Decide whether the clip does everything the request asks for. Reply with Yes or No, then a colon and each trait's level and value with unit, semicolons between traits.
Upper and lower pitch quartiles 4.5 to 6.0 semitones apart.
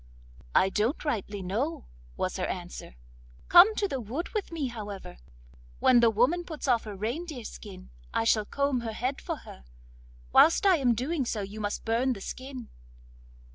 Yes: wide, 5.6 semitones